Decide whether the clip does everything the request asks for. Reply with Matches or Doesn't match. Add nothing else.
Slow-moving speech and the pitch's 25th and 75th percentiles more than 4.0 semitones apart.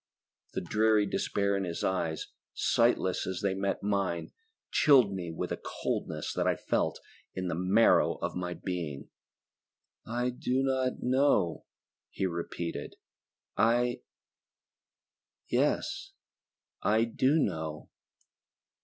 Matches